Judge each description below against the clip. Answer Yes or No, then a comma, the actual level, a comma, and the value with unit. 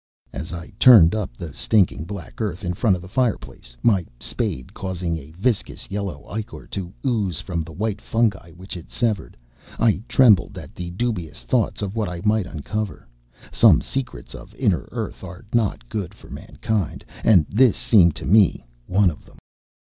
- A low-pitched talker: Yes, very low, 95 Hz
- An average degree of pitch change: Yes, average, 4.3 semitones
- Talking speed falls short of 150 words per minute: No, average, 175 wpm